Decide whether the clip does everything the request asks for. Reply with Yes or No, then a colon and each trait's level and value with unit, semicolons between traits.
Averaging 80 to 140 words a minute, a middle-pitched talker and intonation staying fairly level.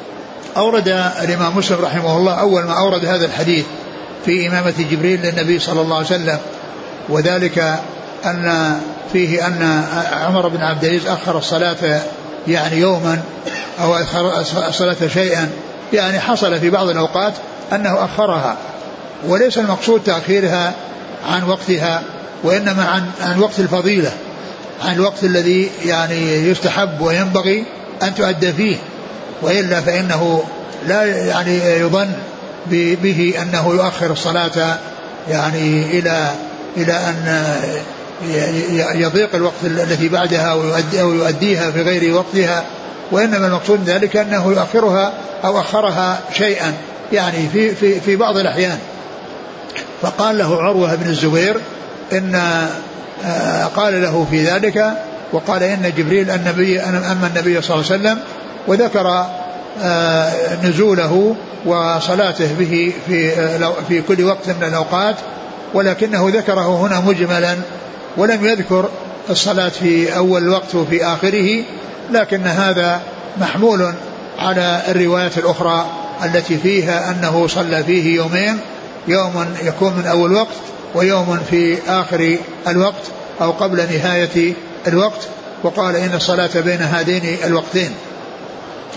Yes: average, 115 wpm; medium, 175 Hz; narrow, 2.3 semitones